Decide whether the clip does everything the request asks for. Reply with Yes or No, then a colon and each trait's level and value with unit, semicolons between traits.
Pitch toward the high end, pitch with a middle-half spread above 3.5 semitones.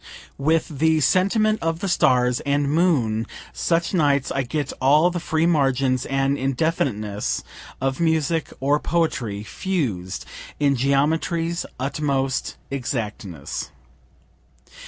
No: medium, 140 Hz; average, 4.1 semitones